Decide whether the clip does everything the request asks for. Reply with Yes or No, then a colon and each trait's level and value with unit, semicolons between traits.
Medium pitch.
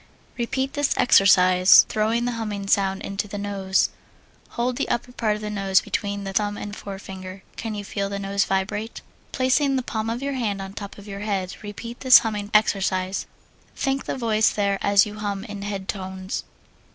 No: high, 205 Hz